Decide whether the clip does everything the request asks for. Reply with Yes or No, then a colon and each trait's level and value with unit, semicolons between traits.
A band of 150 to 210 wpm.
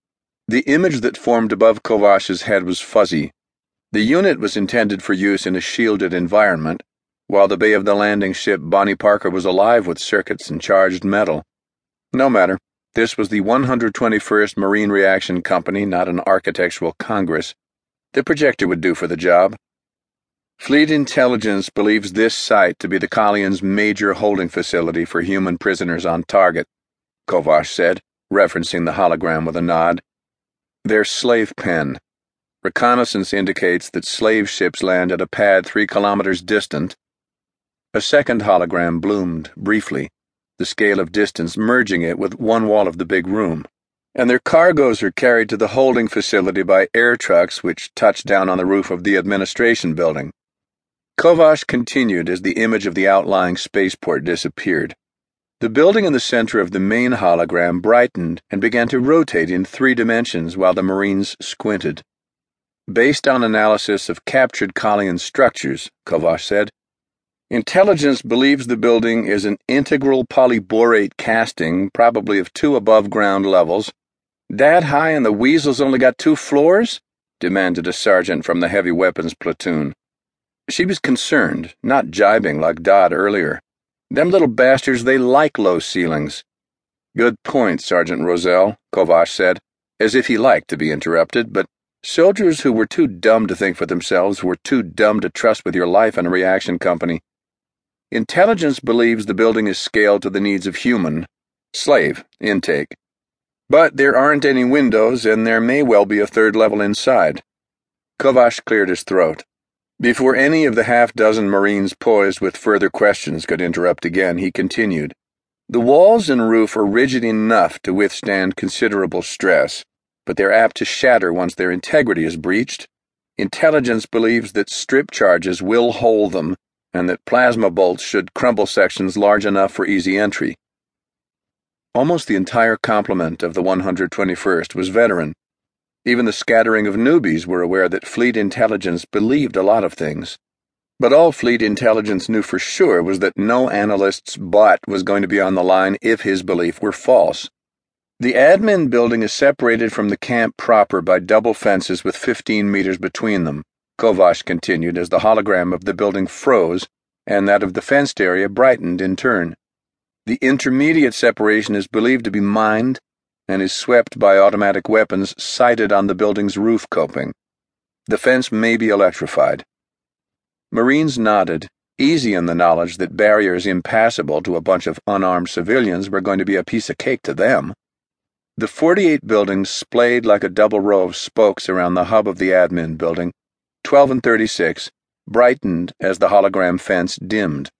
Yes: average, 160 wpm